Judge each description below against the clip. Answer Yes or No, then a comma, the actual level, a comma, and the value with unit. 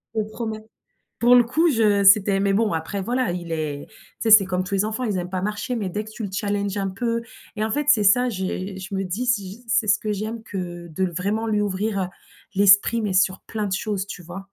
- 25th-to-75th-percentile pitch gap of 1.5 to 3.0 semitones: Yes, average, 2.7 semitones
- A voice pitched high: Yes, high, 205 Hz